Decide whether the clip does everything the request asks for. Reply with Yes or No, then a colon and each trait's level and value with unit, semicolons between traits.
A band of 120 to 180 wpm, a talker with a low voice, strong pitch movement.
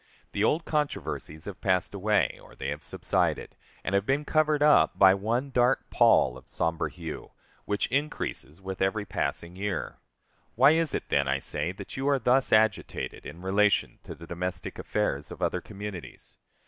Yes: average, 175 wpm; low, 100 Hz; wide, 6.8 semitones